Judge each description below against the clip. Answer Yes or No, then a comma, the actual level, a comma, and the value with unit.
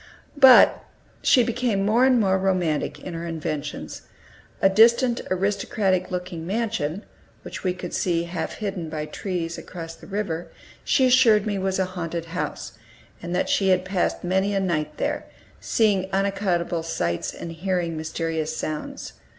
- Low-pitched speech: No, medium, 185 Hz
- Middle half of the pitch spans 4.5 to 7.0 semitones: No, average, 3.2 semitones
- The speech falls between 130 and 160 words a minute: Yes, average, 150 wpm